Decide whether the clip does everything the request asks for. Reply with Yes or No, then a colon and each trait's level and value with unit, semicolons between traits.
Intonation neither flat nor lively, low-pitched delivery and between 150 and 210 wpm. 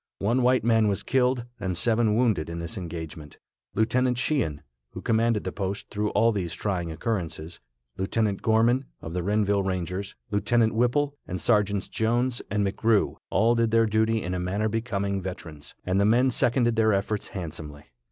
Yes: average, 3.9 semitones; low, 105 Hz; average, 170 wpm